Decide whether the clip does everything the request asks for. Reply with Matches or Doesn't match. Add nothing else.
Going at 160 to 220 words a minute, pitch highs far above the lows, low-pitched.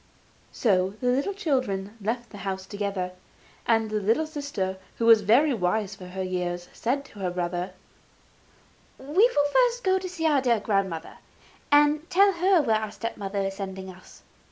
Doesn't match